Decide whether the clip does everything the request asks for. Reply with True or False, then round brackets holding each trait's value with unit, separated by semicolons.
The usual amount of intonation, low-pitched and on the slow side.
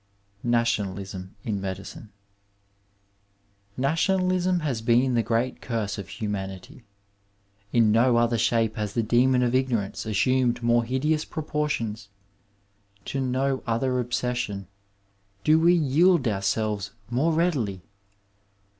True (3.9 semitones; 120 Hz; 110 wpm)